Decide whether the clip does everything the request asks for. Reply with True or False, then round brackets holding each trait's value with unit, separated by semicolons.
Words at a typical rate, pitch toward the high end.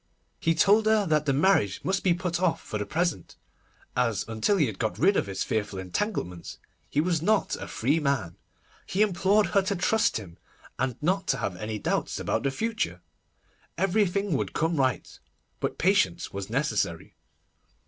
False (175 wpm; 160 Hz)